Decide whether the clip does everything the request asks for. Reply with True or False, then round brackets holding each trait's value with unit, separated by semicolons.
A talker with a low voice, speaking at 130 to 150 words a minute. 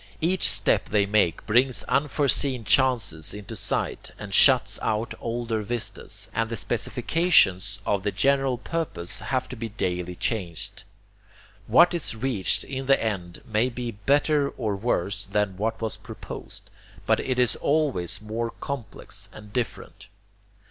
True (115 Hz; 140 wpm)